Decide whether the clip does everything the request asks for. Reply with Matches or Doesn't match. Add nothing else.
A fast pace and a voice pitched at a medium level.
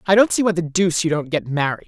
Matches